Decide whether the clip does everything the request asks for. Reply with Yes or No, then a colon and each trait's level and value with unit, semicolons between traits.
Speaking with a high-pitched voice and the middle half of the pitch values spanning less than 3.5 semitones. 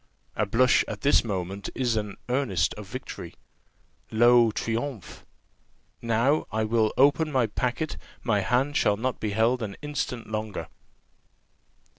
No: low, 115 Hz; average, 3.1 semitones